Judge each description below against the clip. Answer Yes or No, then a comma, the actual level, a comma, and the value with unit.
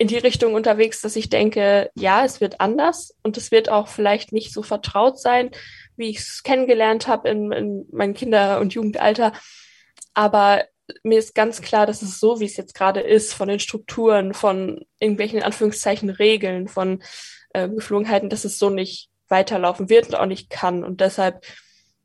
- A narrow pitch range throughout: Yes, narrow, 1.9 semitones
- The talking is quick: No, average, 180 wpm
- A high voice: Yes, high, 210 Hz